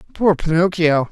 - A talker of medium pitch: Yes, medium, 165 Hz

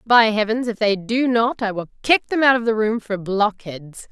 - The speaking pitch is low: No, high, 220 Hz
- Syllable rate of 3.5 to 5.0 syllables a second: Yes, 4.8 syllables/s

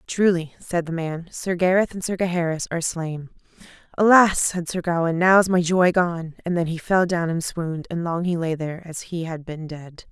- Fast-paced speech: Yes, fast, 220 wpm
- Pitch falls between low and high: Yes, medium, 170 Hz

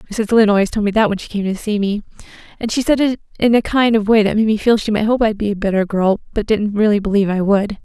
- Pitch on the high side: Yes, high, 210 Hz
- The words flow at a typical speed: No, fast, 300 wpm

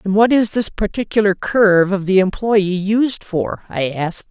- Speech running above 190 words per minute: No, average, 180 wpm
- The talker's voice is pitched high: Yes, high, 200 Hz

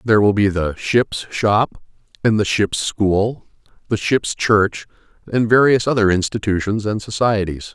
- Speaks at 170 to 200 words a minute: No, average, 145 wpm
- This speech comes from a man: Yes, male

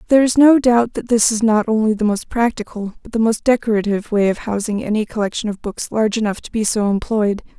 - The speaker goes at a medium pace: No, fast, 230 wpm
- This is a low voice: No, high, 220 Hz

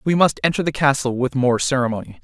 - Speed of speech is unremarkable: No, fast, 215 wpm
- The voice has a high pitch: No, low, 135 Hz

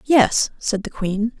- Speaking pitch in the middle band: No, high, 225 Hz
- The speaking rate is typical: Yes, average, 170 wpm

